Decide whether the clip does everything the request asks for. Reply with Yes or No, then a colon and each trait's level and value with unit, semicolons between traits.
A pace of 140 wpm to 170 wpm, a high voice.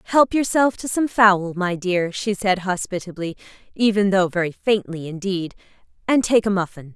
Yes: average, 165 wpm; high, 195 Hz